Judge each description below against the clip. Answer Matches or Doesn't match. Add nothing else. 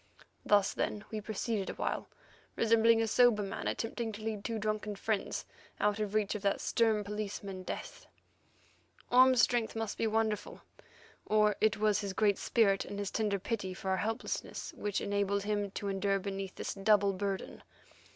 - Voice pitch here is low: Doesn't match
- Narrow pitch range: Matches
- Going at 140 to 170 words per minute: Matches